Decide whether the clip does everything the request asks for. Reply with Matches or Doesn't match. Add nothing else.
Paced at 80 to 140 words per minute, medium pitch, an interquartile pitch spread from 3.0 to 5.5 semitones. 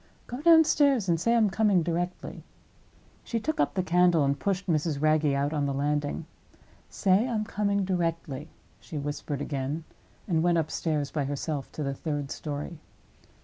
Doesn't match